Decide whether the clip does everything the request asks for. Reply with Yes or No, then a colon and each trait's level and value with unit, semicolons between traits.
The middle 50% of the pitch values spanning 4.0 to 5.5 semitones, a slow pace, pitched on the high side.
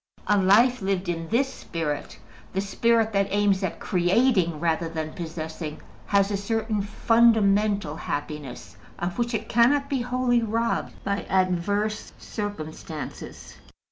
Yes: average, 5.0 semitones; slow, 130 wpm; high, 200 Hz